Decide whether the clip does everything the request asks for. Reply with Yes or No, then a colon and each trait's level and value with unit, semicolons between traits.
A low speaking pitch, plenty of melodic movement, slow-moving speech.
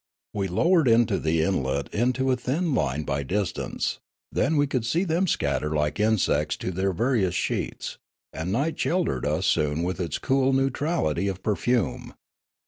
No: low, 105 Hz; wide, 9.0 semitones; average, 160 wpm